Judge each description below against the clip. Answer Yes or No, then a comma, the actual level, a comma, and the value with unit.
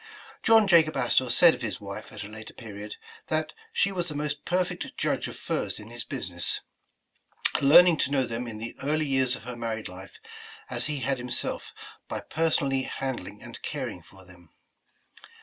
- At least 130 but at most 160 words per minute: No, average, 180 wpm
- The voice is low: Yes, low, 130 Hz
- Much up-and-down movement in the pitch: Yes, wide, 5.9 semitones